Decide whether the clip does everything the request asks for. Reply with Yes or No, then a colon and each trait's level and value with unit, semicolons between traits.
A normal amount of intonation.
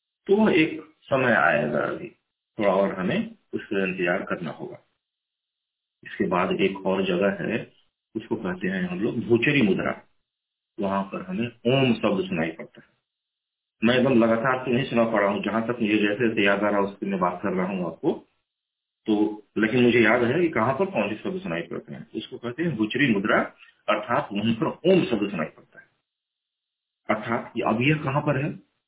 No: wide, 6.0 semitones